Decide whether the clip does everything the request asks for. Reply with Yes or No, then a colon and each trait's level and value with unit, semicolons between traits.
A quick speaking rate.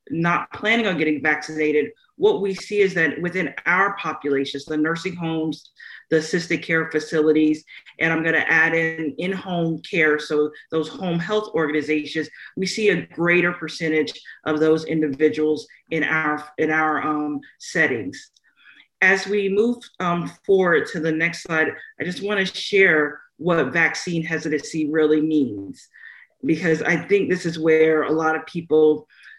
No: average, 155 wpm